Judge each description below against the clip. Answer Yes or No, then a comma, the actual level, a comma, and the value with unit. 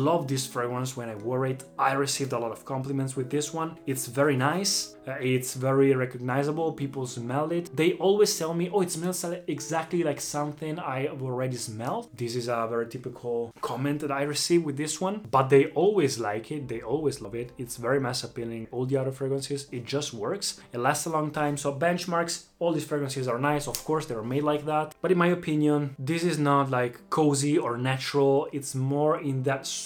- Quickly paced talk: Yes, fast, 210 wpm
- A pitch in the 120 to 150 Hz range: Yes, medium, 140 Hz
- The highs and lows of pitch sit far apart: No, average, 3.3 semitones